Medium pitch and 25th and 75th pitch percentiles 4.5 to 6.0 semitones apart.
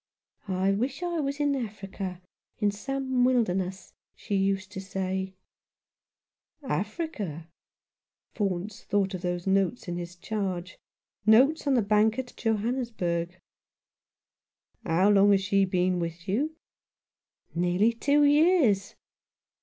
No: high, 200 Hz; average, 4.9 semitones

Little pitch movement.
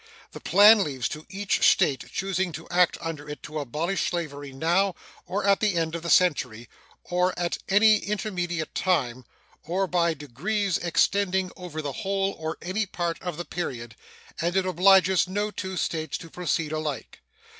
No: average, 3.6 semitones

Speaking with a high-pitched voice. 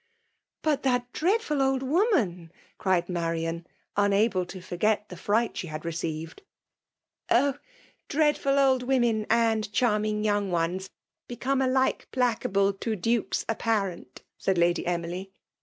Yes: high, 215 Hz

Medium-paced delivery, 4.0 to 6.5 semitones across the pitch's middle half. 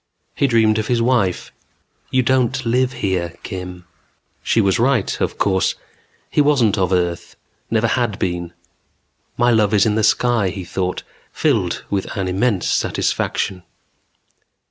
Yes: average, 145 wpm; average, 4.5 semitones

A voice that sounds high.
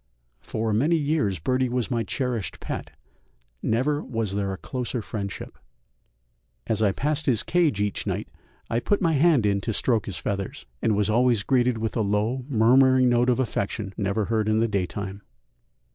No: low, 115 Hz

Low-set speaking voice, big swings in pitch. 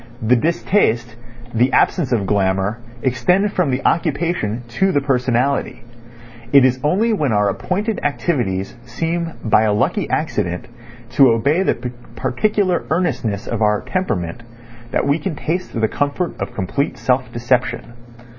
Yes: low, 130 Hz; wide, 6.7 semitones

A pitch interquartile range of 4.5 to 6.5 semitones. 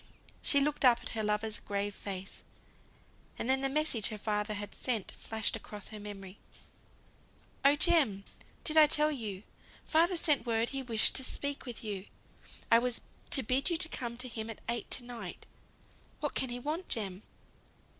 Yes: average, 5.0 semitones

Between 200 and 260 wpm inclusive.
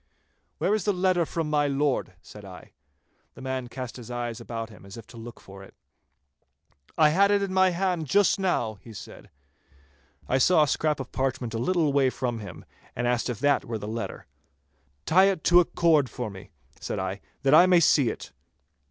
Yes: fast, 205 wpm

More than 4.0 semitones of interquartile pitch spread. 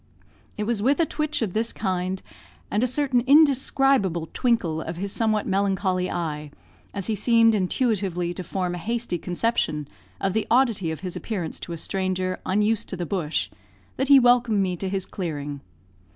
Yes: average, 4.6 semitones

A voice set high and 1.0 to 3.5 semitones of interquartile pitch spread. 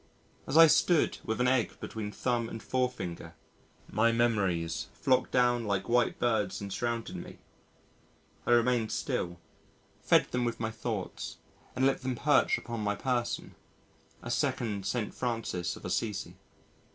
No: low, 115 Hz; average, 3.2 semitones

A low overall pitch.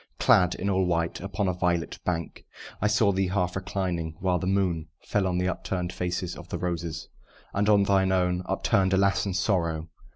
Yes: very low, 90 Hz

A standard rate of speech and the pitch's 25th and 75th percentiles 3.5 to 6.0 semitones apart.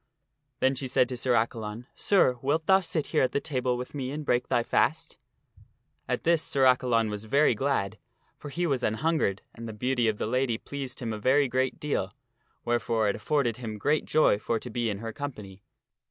No: fast, 210 wpm; average, 4.0 semitones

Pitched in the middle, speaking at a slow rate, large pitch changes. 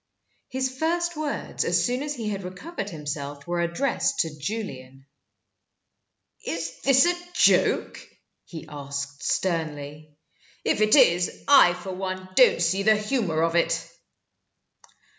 Yes: medium, 180 Hz; slow, 130 wpm; wide, 8.2 semitones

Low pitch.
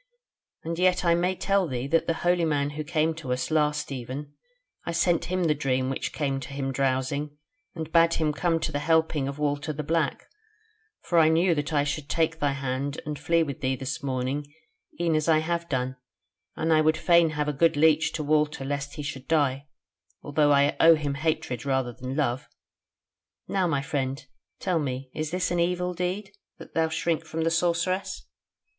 No: medium, 150 Hz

